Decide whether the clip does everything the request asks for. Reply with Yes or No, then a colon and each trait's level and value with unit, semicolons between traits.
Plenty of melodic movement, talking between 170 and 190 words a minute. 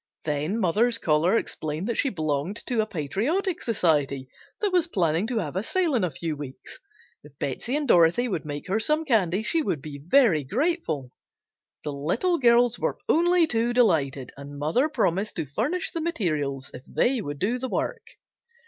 Yes: wide, 8.9 semitones; average, 180 wpm